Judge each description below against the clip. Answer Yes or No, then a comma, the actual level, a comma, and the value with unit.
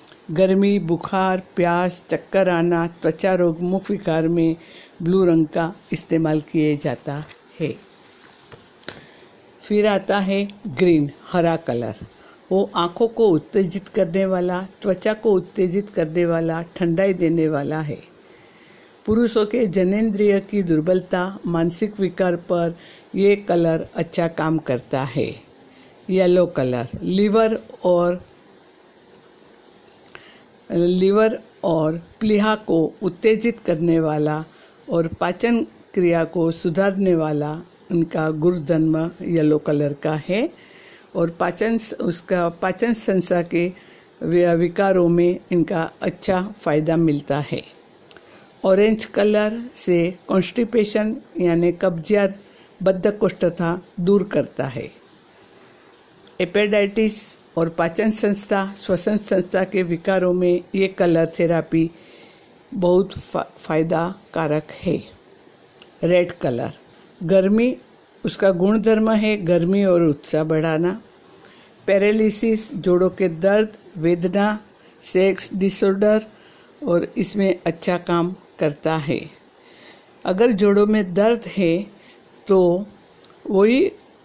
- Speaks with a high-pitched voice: No, medium, 180 Hz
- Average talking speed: No, slow, 100 wpm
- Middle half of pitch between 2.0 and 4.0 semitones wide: Yes, average, 3.2 semitones